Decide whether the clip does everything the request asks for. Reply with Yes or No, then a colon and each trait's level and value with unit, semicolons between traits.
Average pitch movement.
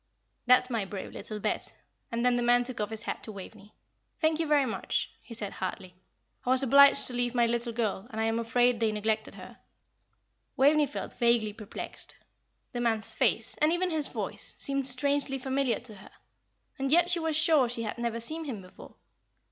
Yes: average, 3.8 semitones